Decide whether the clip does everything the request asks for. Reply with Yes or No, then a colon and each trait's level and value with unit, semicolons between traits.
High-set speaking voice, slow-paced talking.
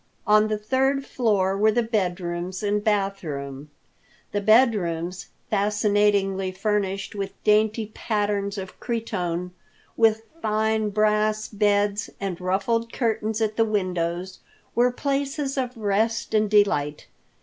Yes: high, 210 Hz; slow, 125 wpm